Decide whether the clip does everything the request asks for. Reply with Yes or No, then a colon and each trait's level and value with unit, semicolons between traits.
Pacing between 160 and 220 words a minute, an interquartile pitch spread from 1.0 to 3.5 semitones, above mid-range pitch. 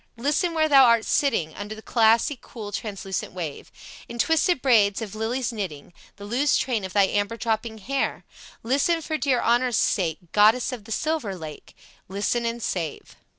No: average, 170 wpm; average, 4.2 semitones; high, 225 Hz